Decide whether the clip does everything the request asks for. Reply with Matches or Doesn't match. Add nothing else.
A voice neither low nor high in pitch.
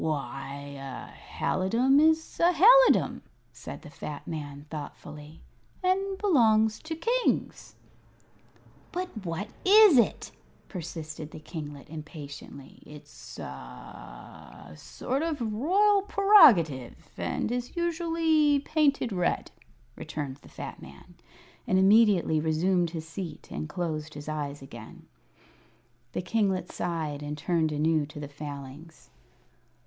Matches